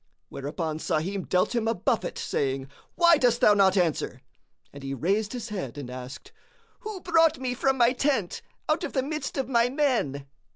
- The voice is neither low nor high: No, high, 220 Hz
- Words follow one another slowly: No, average, 180 wpm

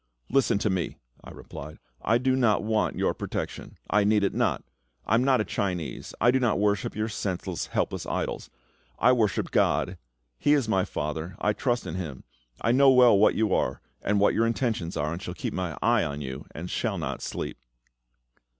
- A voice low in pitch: Yes, low, 105 Hz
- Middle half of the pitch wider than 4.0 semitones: Yes, average, 4.8 semitones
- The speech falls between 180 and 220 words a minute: Yes, average, 195 wpm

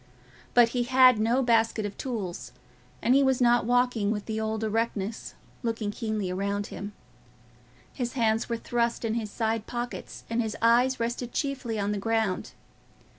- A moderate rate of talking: Yes, average, 165 wpm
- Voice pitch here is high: Yes, high, 230 Hz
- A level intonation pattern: Yes, narrow, 2.0 semitones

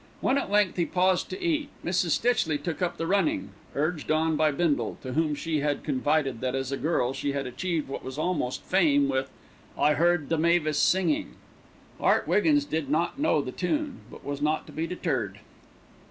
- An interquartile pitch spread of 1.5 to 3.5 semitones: No, average, 4.3 semitones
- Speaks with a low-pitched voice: No, medium, 160 Hz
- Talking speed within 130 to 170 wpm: No, average, 195 wpm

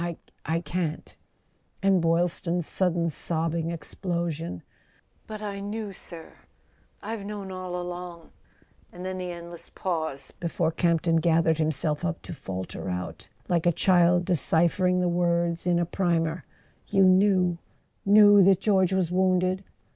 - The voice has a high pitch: No, medium, 175 Hz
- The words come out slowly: No, average, 145 wpm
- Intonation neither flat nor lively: No, narrow, 2.0 semitones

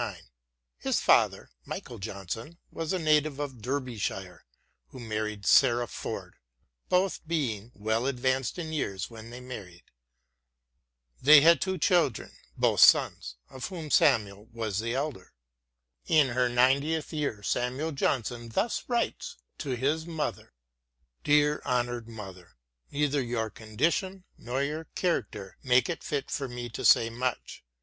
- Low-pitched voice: Yes, low, 125 Hz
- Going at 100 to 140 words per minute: Yes, slow, 135 wpm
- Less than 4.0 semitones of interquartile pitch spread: No, average, 5.1 semitones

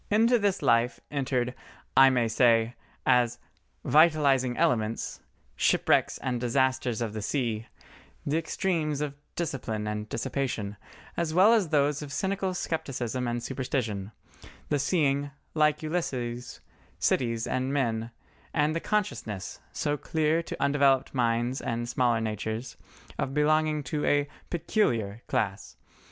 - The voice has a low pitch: Yes, low, 130 Hz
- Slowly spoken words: Yes, slow, 125 wpm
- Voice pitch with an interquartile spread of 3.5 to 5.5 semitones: Yes, average, 4.6 semitones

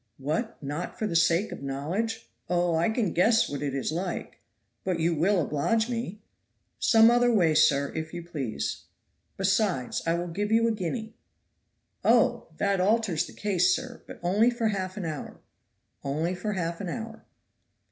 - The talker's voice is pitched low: No, medium, 185 Hz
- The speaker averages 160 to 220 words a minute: Yes, average, 170 wpm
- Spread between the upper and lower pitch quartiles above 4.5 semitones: Yes, average, 5.3 semitones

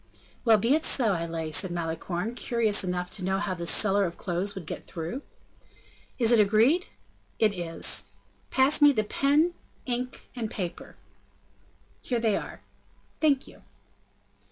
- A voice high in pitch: Yes, high, 210 Hz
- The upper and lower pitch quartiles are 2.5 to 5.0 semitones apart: No, wide, 5.6 semitones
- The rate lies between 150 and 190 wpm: Yes, average, 155 wpm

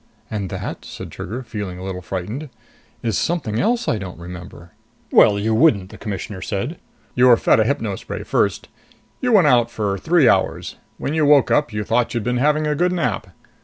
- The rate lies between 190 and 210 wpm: Yes, average, 200 wpm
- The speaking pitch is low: Yes, low, 115 Hz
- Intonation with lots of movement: Yes, wide, 7.0 semitones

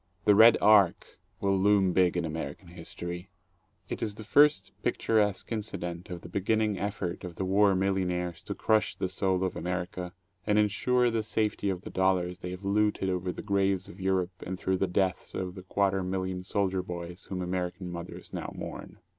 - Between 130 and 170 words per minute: No, average, 190 wpm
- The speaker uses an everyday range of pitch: No, narrow, 2.2 semitones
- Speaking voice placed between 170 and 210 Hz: No, very low, 95 Hz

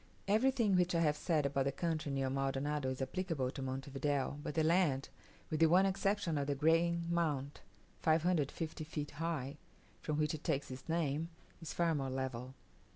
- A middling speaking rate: Yes, average, 180 wpm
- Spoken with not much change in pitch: No, average, 3.5 semitones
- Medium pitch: Yes, medium, 150 Hz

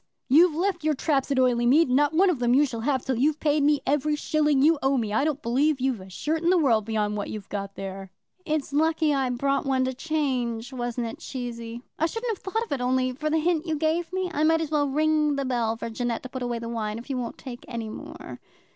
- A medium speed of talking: No, fast, 260 wpm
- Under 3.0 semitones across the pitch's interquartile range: No, average, 4.4 semitones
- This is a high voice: Yes, very high, 270 Hz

